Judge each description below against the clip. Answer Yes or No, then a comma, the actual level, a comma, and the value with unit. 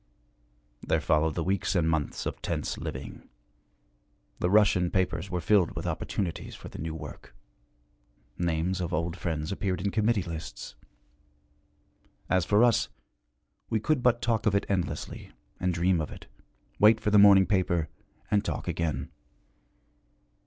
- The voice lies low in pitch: Yes, very low, 90 Hz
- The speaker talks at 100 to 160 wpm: Yes, average, 145 wpm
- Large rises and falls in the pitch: No, average, 3.8 semitones